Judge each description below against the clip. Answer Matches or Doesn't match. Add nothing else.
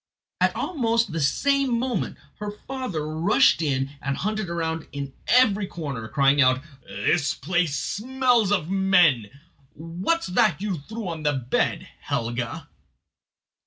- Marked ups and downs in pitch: Matches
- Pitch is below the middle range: Doesn't match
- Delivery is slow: Matches